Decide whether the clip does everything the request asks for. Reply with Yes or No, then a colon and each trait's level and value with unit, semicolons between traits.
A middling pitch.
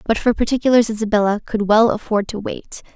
No: high, 215 Hz